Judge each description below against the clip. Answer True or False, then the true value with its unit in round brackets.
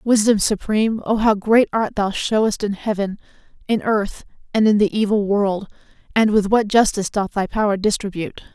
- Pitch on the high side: True (210 Hz)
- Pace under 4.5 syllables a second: False (5.2 syllables/s)